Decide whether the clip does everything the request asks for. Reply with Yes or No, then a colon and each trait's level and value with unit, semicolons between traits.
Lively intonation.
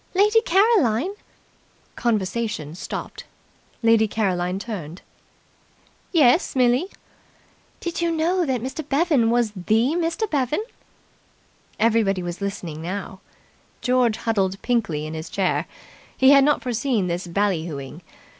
Yes: wide, 6.9 semitones